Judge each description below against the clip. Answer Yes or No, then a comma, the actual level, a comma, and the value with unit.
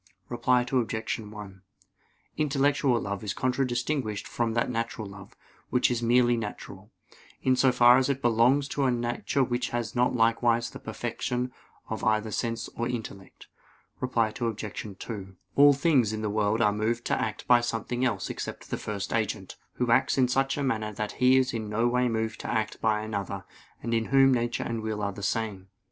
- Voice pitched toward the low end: Yes, low, 115 Hz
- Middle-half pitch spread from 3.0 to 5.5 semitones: No, narrow, 2.6 semitones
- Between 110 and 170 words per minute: No, average, 185 wpm